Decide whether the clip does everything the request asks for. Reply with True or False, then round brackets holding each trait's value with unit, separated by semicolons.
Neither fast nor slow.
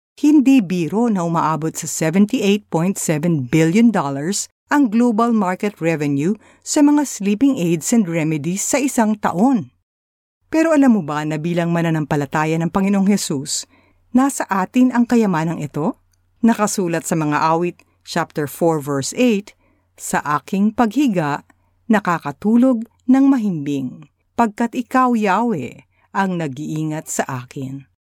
True (120 wpm)